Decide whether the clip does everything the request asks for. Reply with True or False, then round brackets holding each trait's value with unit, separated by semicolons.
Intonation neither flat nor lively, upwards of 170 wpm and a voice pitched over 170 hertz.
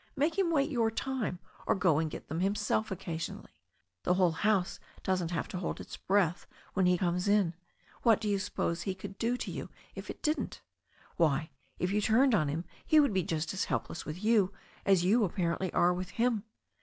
True (4.0 semitones; 205 wpm; 190 Hz)